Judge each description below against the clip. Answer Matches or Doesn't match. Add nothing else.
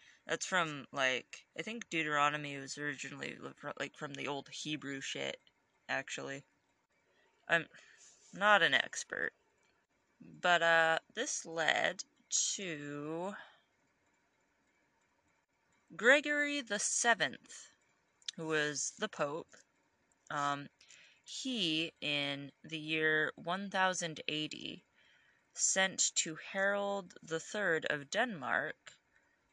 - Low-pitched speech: Doesn't match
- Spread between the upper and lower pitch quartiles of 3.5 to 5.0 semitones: Matches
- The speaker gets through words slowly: Matches